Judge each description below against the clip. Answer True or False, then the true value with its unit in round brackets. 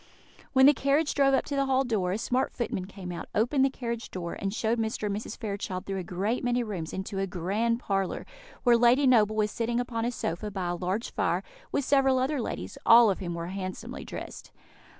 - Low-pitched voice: False (220 Hz)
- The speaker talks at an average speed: False (220 wpm)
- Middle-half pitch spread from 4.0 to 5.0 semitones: True (4.5 semitones)